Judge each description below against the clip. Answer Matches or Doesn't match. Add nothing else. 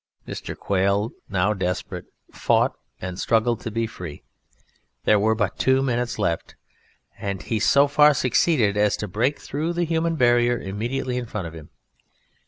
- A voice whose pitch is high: Doesn't match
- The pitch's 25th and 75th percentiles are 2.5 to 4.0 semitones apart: Doesn't match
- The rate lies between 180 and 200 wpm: Doesn't match